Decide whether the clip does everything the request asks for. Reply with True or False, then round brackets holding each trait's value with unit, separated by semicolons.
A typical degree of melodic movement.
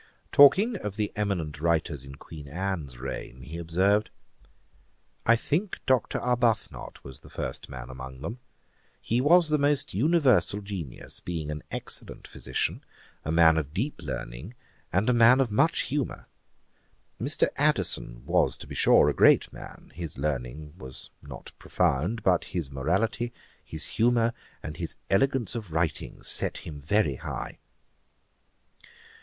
False (8.1 semitones)